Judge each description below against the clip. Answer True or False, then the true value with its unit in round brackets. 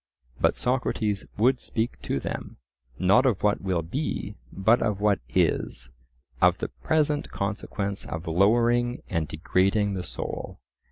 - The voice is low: True (100 Hz)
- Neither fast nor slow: False (130 wpm)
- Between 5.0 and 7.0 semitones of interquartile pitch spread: True (5.6 semitones)